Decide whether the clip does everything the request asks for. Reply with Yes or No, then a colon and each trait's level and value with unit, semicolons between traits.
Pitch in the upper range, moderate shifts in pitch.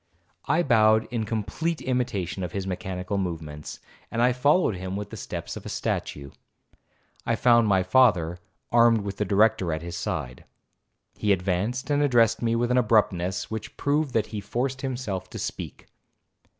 No: low, 110 Hz; average, 4.8 semitones